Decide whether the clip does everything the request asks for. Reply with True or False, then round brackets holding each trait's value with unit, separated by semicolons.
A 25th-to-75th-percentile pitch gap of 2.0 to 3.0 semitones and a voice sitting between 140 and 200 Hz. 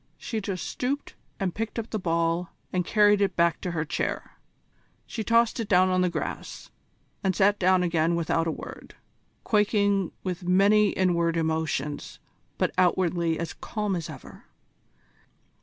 False (3.5 semitones; 185 Hz)